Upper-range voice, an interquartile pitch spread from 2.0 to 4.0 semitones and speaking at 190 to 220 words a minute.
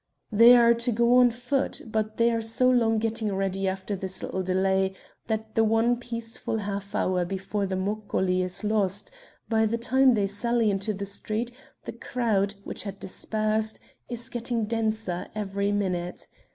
No: high, 215 Hz; average, 3.0 semitones; average, 165 wpm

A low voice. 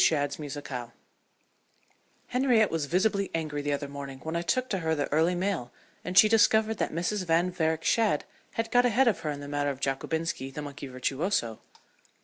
No: medium, 160 Hz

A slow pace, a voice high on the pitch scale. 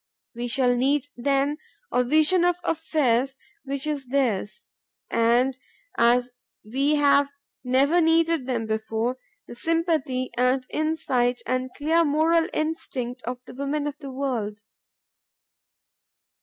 Yes: slow, 120 wpm; very high, 270 Hz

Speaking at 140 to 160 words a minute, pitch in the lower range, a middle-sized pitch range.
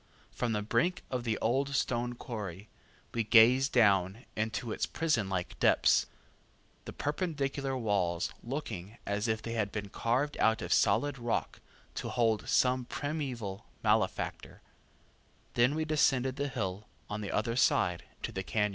Yes: average, 145 wpm; low, 115 Hz; average, 4.4 semitones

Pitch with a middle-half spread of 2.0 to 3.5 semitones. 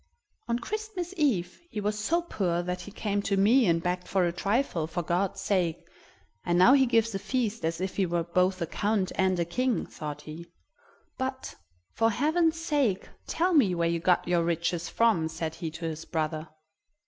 No: wide, 5.5 semitones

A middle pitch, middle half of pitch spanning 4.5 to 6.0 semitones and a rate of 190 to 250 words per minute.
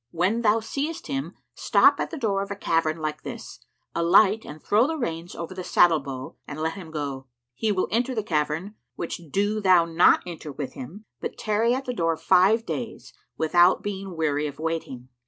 Yes: medium, 180 Hz; average, 5.2 semitones; average, 195 wpm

